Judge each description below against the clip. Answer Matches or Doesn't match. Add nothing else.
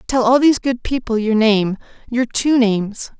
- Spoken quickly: Doesn't match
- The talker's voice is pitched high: Matches